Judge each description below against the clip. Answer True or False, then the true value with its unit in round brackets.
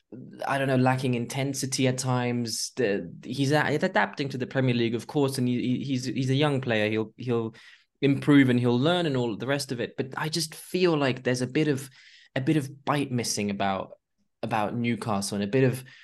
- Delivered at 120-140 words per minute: False (200 wpm)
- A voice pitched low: True (130 Hz)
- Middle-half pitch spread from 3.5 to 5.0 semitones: False (2.8 semitones)